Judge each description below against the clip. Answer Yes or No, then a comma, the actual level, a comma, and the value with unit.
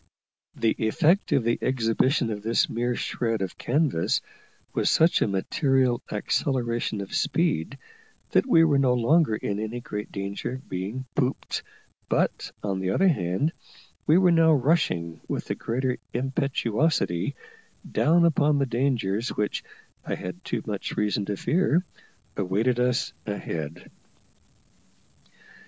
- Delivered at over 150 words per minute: No, slow, 135 wpm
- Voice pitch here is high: No, low, 120 Hz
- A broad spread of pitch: Yes, wide, 5.8 semitones